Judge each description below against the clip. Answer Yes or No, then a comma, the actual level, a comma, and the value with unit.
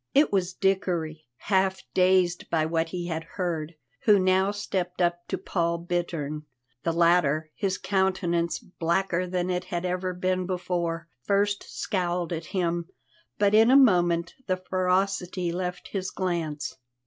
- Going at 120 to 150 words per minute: Yes, average, 145 wpm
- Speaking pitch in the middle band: Yes, medium, 180 Hz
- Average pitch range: No, narrow, 1.8 semitones